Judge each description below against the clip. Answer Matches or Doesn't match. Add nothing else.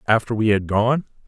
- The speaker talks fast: Doesn't match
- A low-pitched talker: Matches